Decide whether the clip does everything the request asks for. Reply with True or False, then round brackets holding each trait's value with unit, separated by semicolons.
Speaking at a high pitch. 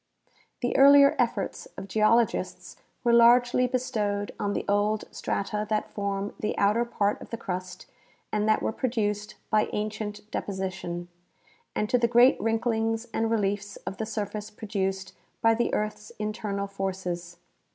True (210 Hz)